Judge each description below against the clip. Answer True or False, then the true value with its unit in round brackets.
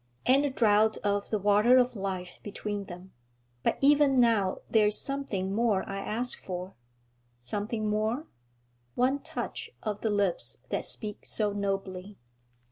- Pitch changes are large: False (3.2 semitones)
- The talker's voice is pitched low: False (210 Hz)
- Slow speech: False (145 wpm)